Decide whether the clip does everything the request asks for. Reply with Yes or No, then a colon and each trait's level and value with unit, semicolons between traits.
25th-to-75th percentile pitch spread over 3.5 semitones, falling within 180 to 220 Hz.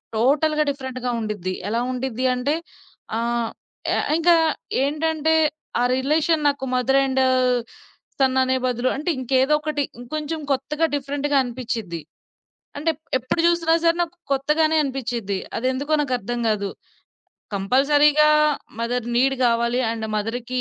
No: average, 3.9 semitones; very high, 265 Hz